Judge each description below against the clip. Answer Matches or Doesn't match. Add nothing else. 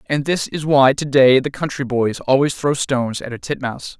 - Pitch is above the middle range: Doesn't match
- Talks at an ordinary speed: Doesn't match